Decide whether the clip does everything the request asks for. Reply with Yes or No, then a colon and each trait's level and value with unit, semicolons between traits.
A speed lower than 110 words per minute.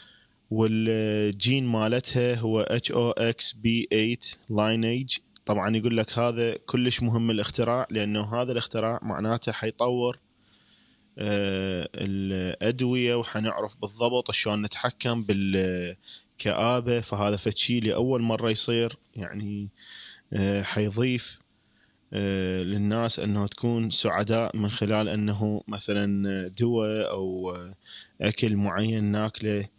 Yes: average, 85 wpm